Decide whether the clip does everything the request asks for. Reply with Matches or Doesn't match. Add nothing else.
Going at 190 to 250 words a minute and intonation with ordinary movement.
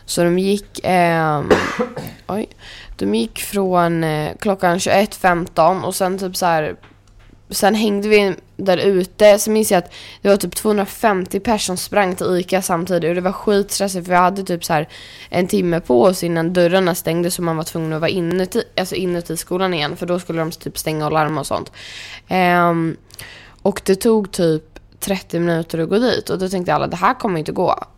Matches